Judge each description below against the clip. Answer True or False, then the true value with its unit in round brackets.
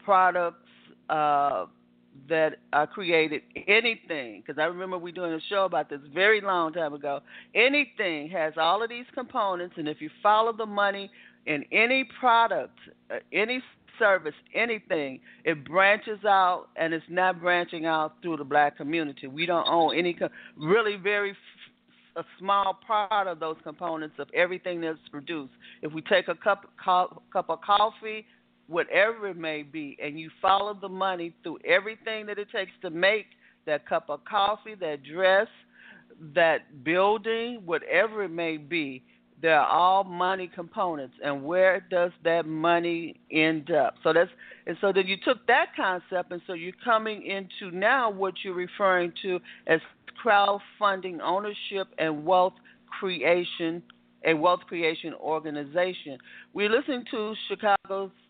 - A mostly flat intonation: False (4.2 semitones)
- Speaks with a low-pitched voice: False (180 Hz)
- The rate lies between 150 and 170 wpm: True (155 wpm)